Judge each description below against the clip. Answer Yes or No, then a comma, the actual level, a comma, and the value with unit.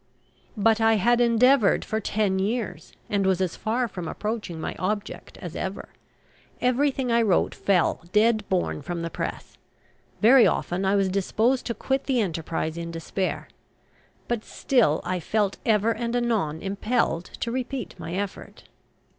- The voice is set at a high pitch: Yes, high, 210 Hz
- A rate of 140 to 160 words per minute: Yes, average, 155 wpm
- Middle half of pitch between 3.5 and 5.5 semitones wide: Yes, average, 4.1 semitones